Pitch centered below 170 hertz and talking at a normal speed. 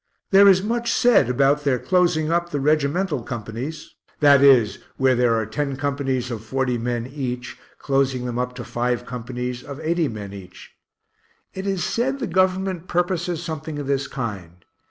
Yes: medium, 140 Hz; average, 170 wpm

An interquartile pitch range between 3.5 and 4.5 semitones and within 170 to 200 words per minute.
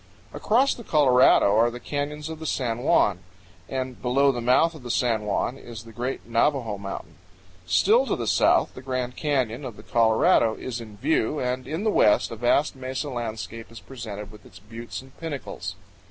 Yes: average, 3.8 semitones; average, 190 wpm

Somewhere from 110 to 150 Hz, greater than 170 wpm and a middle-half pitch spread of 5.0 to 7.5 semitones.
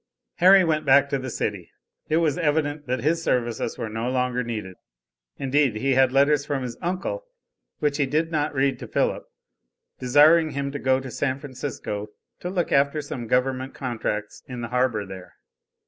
No: low, 135 Hz; average, 180 wpm; average, 3.2 semitones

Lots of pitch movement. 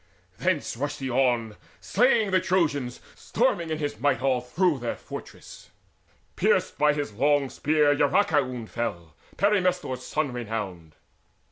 No: average, 5.0 semitones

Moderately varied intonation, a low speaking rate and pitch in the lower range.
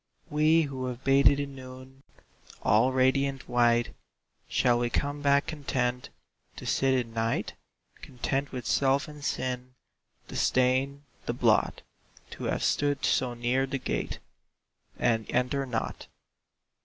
No: narrow, 2.0 semitones; slow, 130 wpm; low, 130 Hz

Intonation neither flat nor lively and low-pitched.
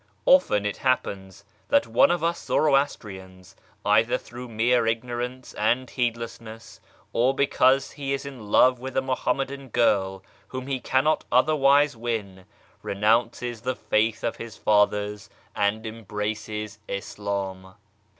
Yes: average, 3.9 semitones; low, 115 Hz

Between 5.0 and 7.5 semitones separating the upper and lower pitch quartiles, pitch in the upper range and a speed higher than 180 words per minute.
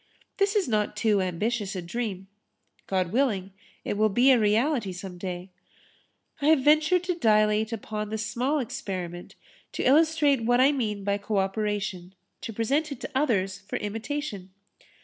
No: wide, 5.4 semitones; high, 215 Hz; average, 160 wpm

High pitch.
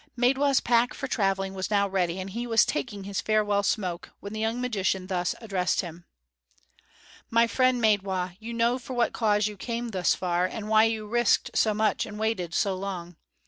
Yes: high, 210 Hz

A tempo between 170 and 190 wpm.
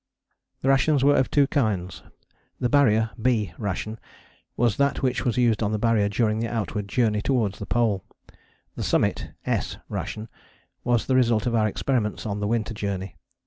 Yes: average, 175 wpm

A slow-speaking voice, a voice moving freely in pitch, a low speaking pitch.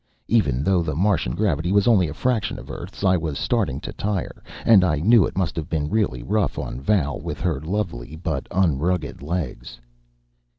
No: average, 185 wpm; wide, 5.7 semitones; very low, 85 Hz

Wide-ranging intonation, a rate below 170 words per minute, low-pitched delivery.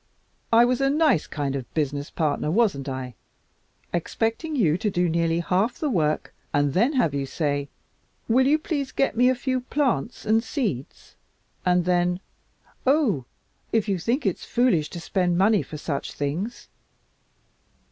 No: wide, 8.4 semitones; average, 160 wpm; medium, 185 Hz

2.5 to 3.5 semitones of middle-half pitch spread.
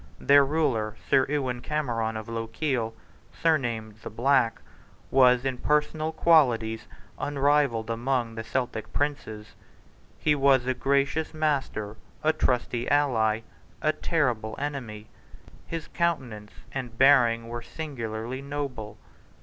No: average, 4.3 semitones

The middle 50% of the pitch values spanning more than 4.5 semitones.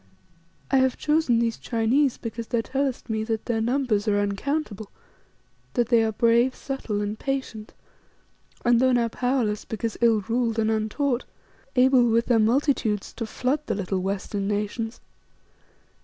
No: average, 2.9 semitones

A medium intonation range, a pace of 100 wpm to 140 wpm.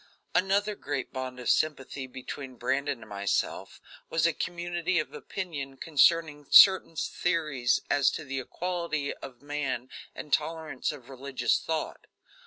Yes: average, 4.0 semitones; slow, 135 wpm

